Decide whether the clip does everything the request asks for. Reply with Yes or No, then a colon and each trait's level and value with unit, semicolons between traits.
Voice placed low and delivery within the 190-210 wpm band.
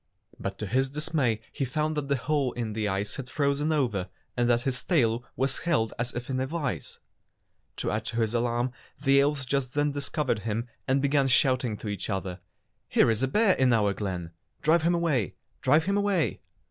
Yes: low, 130 Hz; average, 200 wpm